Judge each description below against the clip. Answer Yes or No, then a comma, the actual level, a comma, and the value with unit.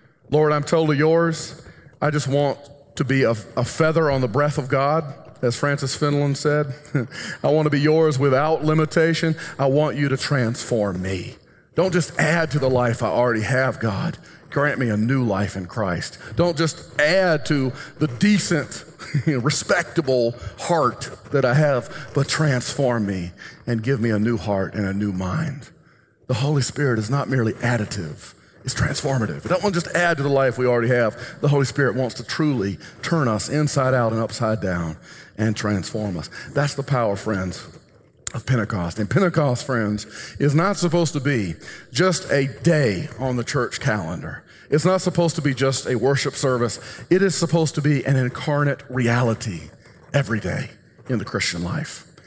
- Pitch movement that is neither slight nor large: Yes, average, 4.6 semitones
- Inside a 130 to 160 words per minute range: No, average, 180 wpm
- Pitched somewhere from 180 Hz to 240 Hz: No, low, 135 Hz